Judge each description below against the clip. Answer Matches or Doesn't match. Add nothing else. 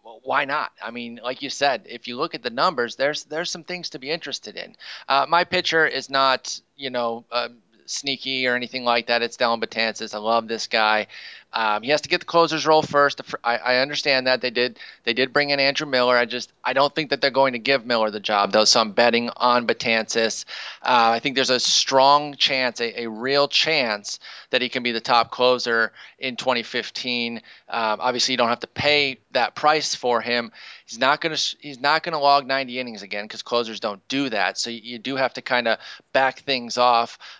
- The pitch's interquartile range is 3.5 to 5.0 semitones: Doesn't match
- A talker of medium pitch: Doesn't match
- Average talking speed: Doesn't match